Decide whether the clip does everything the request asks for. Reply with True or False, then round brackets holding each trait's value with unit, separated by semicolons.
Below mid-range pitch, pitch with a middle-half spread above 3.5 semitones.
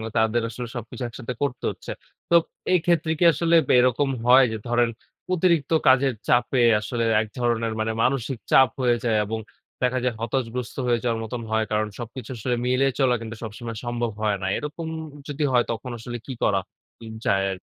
False (120 Hz; 2.8 semitones)